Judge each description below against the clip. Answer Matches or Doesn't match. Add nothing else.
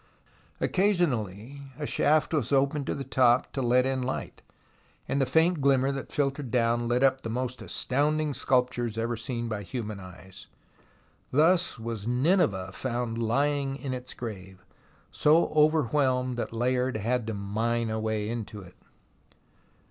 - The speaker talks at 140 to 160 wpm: Matches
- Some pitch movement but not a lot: Matches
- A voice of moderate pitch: Doesn't match